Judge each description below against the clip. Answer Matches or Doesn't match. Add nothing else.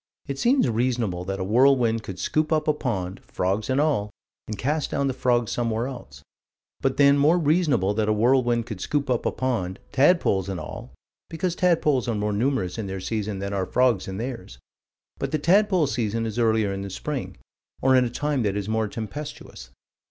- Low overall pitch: Matches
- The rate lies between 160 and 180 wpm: Doesn't match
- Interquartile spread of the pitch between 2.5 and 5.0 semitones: Doesn't match